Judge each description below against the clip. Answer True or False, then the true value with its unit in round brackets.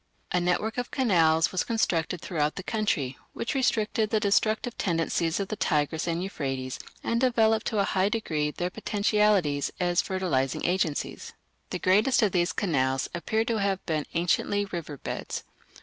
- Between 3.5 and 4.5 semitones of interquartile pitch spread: False (4.9 semitones)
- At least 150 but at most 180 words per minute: True (160 wpm)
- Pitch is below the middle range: False (185 Hz)